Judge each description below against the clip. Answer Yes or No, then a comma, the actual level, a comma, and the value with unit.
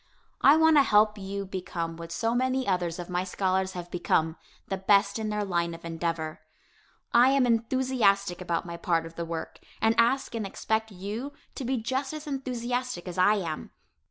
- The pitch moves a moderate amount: No, wide, 5.8 semitones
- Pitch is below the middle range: No, high, 200 Hz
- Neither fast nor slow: Yes, average, 185 wpm